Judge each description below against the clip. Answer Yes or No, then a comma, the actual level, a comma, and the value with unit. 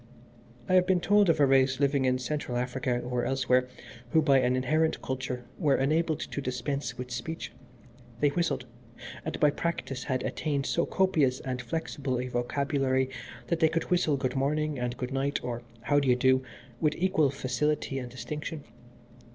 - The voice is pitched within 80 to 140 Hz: Yes, low, 135 Hz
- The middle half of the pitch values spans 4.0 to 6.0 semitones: No, average, 3.2 semitones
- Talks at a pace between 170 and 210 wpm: Yes, average, 175 wpm